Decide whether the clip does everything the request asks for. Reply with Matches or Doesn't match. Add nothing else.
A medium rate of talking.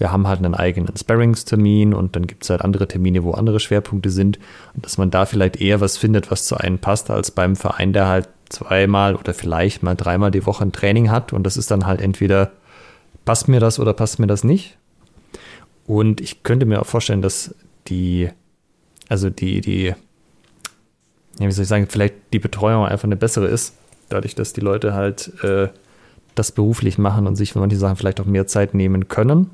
Doesn't match